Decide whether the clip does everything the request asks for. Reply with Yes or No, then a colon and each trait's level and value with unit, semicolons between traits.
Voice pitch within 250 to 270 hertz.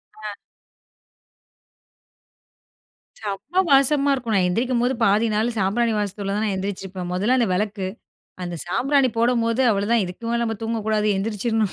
No: high, 220 Hz